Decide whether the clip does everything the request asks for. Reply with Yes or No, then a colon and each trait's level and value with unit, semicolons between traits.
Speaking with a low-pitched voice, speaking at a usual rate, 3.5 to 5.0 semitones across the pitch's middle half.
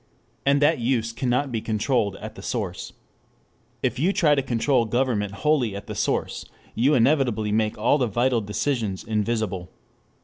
Yes: low, 120 Hz; average, 160 wpm; average, 4.1 semitones